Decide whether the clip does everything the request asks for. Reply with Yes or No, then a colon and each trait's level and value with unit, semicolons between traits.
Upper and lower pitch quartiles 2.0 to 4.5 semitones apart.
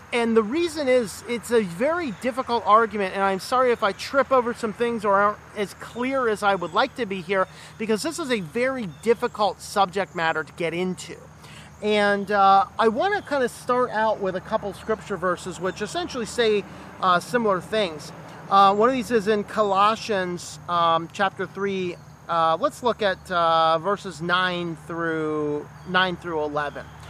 No: average, 4.9 semitones